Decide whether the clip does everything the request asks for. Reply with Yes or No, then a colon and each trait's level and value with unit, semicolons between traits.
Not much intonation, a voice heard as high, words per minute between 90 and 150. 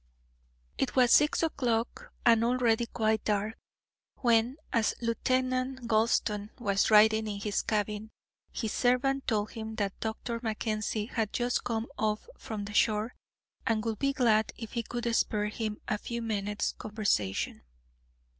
Yes: narrow, 2.2 semitones; high, 225 Hz; average, 145 wpm